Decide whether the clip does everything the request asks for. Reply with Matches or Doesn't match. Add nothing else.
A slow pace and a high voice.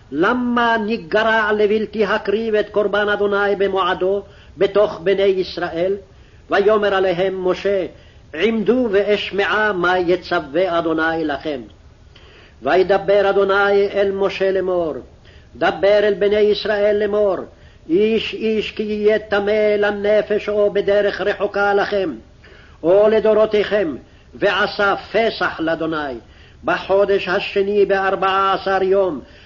Matches